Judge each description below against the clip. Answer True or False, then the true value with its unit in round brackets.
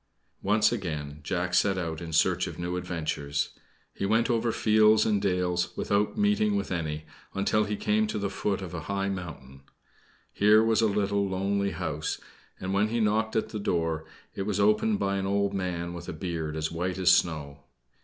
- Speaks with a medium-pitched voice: False (95 Hz)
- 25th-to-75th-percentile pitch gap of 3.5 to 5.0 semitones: True (3.8 semitones)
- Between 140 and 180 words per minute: False (190 wpm)